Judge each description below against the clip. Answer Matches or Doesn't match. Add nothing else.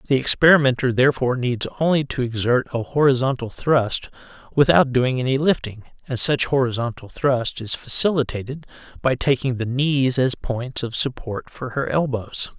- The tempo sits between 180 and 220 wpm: Doesn't match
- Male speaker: Matches